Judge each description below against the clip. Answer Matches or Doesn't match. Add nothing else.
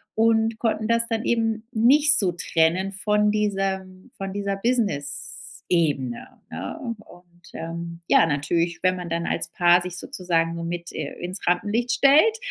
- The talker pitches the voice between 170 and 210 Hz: Matches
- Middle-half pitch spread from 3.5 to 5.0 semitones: Matches